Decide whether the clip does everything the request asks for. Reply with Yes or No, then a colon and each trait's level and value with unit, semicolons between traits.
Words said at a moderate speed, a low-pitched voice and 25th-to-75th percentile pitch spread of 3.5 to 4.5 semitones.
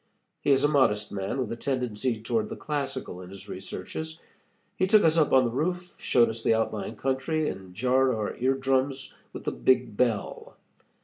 Yes: average, 190 wpm; low, 130 Hz; average, 4.0 semitones